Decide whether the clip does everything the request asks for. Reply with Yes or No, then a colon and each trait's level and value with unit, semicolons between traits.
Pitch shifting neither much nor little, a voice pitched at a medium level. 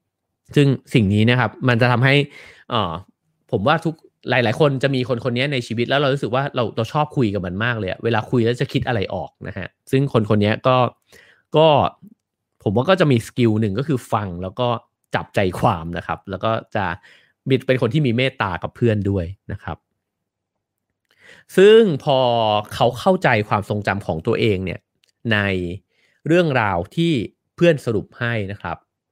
No: average, 4.5 semitones; low, 120 Hz